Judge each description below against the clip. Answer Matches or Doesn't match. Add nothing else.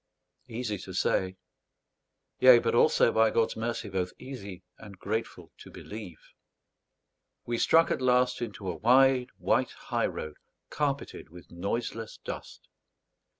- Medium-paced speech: Doesn't match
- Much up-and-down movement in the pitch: Doesn't match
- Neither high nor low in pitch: Doesn't match